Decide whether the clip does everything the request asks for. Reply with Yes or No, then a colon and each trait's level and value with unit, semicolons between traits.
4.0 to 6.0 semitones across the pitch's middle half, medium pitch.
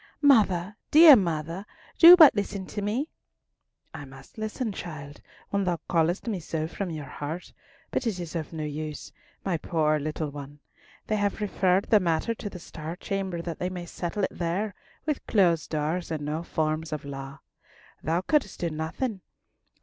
Yes: average, 4.6 semitones; medium, 175 Hz